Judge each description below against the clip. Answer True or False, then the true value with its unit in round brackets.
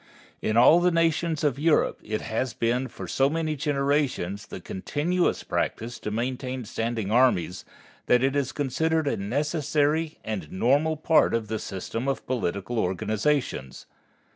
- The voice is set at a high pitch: False (130 Hz)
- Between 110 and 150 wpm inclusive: True (145 wpm)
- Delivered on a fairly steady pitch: False (5.3 semitones)